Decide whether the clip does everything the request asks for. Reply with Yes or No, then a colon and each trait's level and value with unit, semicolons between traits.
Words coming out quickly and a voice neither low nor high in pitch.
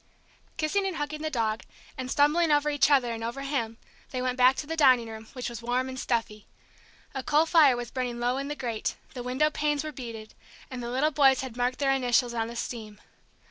No: fast, 220 wpm; very high, 255 Hz